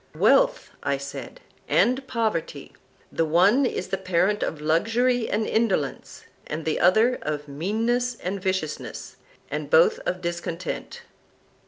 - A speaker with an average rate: No, slow, 130 wpm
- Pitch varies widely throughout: Yes, wide, 6.1 semitones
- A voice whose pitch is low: No, medium, 185 Hz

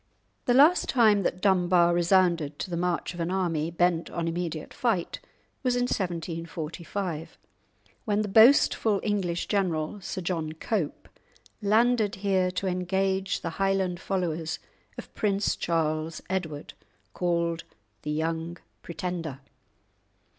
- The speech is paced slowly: Yes, slow, 125 wpm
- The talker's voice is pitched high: No, medium, 180 Hz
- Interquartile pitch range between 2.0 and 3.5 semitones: Yes, average, 2.9 semitones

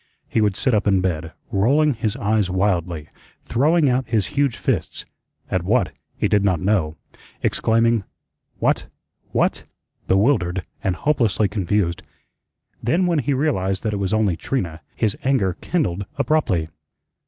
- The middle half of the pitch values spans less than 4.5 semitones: No, wide, 5.6 semitones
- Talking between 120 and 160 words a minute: Yes, average, 145 wpm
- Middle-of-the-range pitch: No, low, 105 Hz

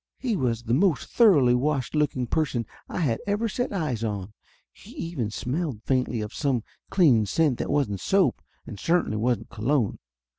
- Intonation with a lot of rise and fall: Yes, wide, 6.1 semitones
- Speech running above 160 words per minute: Yes, average, 170 wpm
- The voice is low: Yes, low, 130 Hz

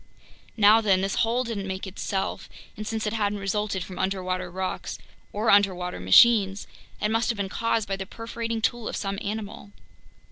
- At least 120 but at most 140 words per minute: No, average, 175 wpm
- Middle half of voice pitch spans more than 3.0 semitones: No, narrow, 2.6 semitones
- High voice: Yes, high, 205 Hz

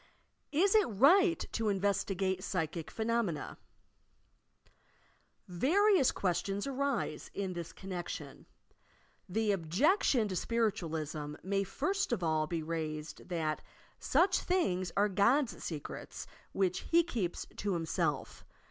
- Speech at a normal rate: No, slow, 110 wpm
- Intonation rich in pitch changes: Yes, wide, 7.1 semitones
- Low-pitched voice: No, high, 195 Hz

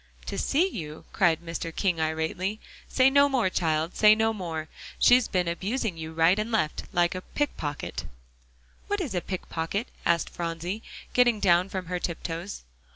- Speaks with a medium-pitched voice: Yes, medium, 180 Hz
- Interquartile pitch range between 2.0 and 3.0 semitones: No, average, 4.9 semitones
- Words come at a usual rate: Yes, average, 170 wpm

